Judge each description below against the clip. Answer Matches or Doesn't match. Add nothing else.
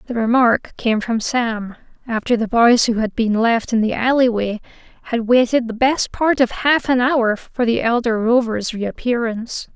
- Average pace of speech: Matches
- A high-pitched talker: Matches